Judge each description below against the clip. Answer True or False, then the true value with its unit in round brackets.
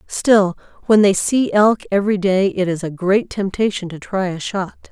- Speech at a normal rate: True (195 wpm)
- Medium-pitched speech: False (195 Hz)